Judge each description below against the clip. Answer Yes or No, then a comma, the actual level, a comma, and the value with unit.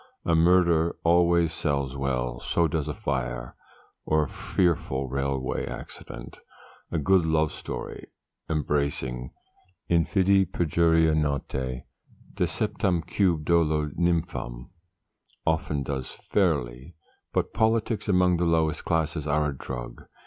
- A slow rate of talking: Yes, slow, 110 wpm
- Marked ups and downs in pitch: No, average, 3.9 semitones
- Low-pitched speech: Yes, very low, 80 Hz